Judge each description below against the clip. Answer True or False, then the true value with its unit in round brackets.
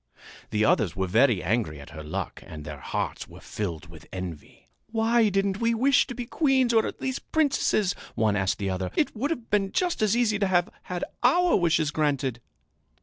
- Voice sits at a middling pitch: True (175 Hz)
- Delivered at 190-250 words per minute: True (200 wpm)